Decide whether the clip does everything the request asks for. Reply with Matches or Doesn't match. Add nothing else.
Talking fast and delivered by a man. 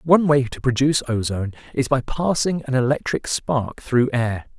Doesn't match